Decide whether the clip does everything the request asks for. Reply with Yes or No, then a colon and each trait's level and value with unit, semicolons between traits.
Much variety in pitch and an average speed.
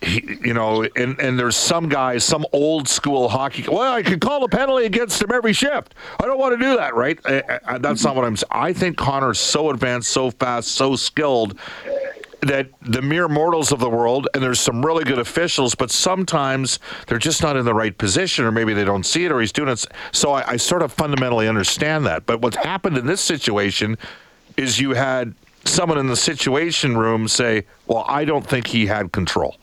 No: wide, 5.7 semitones; fast, 215 wpm